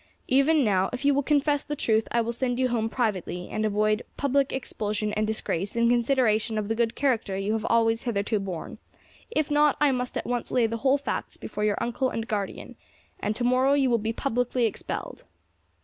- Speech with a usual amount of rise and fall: Yes, average, 3.6 semitones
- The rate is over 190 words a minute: Yes, fast, 205 wpm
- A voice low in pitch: No, high, 235 Hz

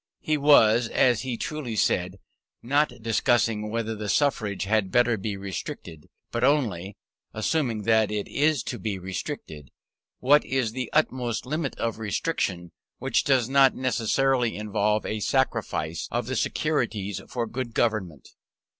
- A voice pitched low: Yes, low, 115 Hz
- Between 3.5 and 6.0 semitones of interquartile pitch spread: Yes, average, 3.8 semitones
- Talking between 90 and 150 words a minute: Yes, average, 140 wpm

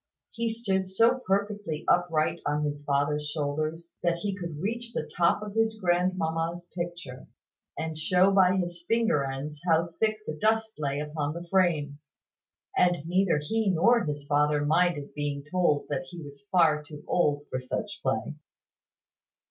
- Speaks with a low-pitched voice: No, medium, 170 Hz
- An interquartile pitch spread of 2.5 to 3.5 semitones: No, average, 4.3 semitones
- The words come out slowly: No, average, 155 wpm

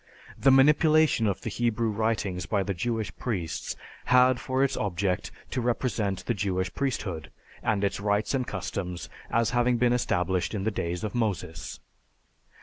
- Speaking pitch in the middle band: No, low, 110 Hz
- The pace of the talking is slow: No, average, 155 wpm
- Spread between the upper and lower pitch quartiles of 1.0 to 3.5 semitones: No, average, 4.5 semitones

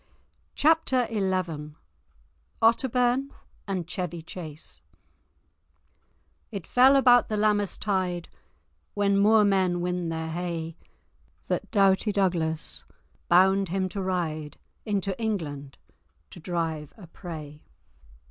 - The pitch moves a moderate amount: Yes, average, 4.0 semitones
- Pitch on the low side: No, medium, 185 Hz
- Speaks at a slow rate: Yes, slow, 100 wpm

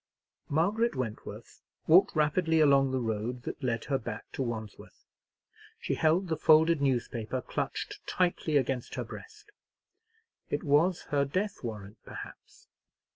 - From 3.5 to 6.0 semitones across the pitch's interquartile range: Yes, average, 5.3 semitones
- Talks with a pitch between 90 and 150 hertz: Yes, medium, 140 Hz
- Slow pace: Yes, slow, 130 wpm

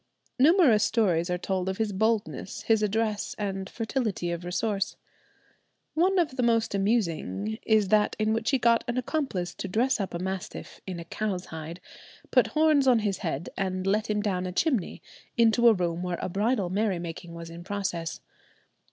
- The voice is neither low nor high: No, high, 200 Hz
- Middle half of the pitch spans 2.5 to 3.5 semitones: No, average, 4.2 semitones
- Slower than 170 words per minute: No, average, 180 wpm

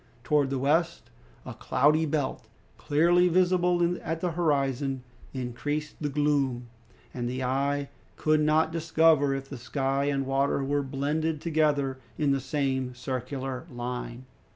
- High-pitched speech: No, medium, 140 Hz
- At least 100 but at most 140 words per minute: Yes, slow, 135 wpm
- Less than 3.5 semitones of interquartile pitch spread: Yes, average, 2.8 semitones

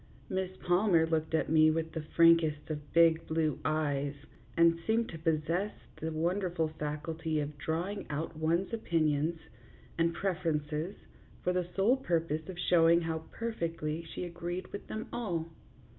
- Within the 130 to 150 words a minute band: Yes, average, 145 wpm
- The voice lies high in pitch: No, medium, 165 Hz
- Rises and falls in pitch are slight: Yes, narrow, 2.2 semitones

